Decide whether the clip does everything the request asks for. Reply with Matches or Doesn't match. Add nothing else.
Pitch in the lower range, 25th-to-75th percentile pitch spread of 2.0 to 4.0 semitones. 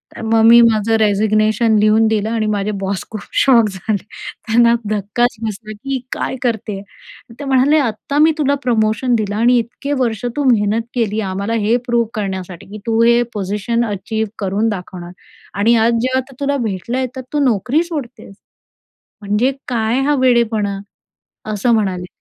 Doesn't match